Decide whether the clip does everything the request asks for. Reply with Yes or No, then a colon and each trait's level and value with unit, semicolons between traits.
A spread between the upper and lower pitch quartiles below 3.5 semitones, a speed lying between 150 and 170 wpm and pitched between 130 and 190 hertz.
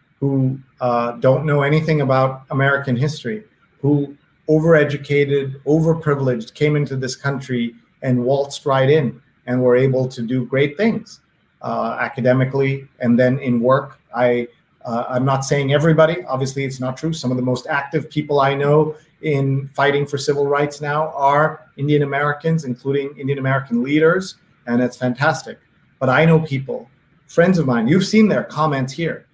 Yes: average, 2.9 semitones; average, 160 wpm; medium, 140 Hz